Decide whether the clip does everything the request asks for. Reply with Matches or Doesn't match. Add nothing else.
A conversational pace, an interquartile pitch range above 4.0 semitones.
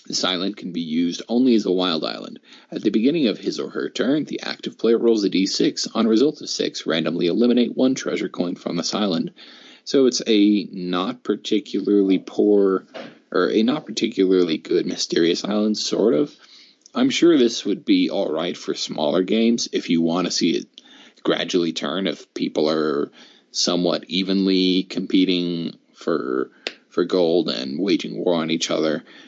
Matches